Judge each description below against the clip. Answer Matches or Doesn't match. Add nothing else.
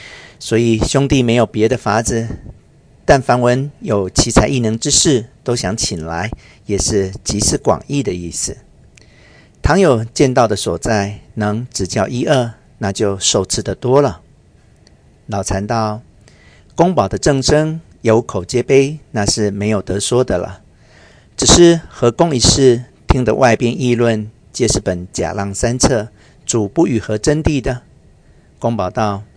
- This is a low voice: Matches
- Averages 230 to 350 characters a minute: Doesn't match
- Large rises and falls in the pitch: Doesn't match